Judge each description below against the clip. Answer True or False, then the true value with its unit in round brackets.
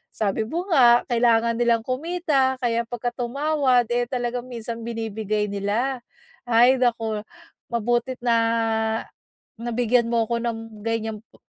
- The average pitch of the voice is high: True (235 Hz)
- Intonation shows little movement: True (1.6 semitones)